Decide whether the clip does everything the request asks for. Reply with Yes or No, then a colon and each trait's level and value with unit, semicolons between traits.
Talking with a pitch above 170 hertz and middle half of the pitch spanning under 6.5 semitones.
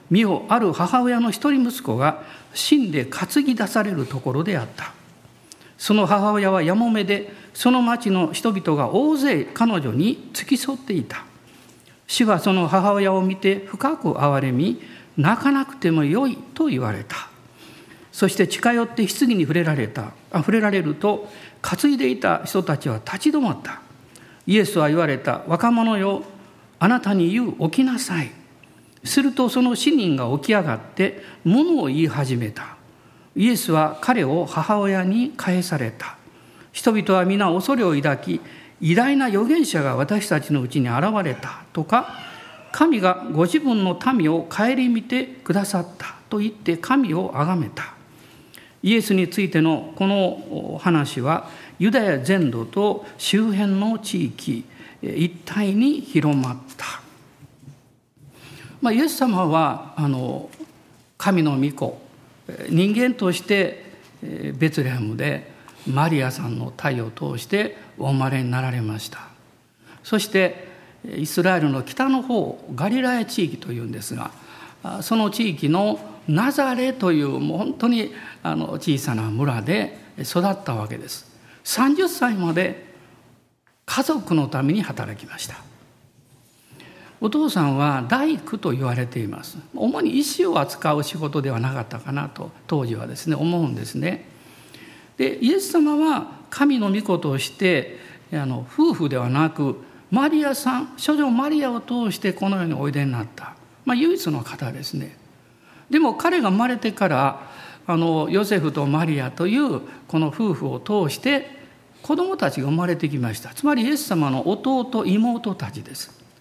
No: medium, 185 Hz; wide, 8.3 semitones